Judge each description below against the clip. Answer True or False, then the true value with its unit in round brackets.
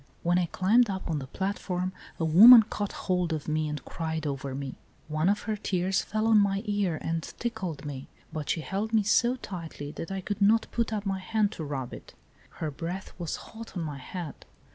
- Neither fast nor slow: False (210 wpm)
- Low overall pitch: False (180 Hz)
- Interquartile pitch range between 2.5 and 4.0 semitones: False (4.8 semitones)